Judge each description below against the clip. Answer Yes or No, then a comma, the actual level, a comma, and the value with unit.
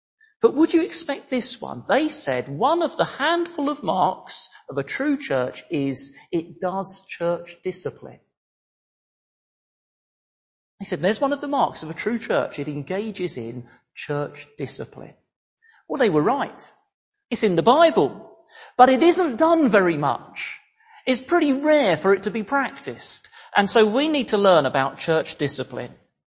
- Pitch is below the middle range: No, high, 220 Hz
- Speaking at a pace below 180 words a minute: Yes, average, 160 wpm